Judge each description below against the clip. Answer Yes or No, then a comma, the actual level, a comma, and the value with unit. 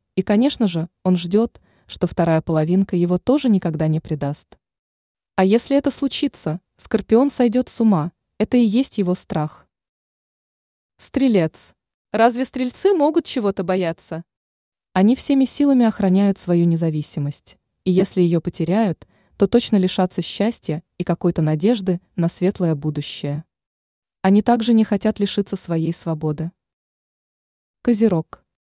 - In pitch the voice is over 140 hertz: Yes, medium, 185 Hz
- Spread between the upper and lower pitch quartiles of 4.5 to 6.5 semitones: Yes, wide, 5.6 semitones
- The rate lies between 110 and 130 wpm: Yes, average, 125 wpm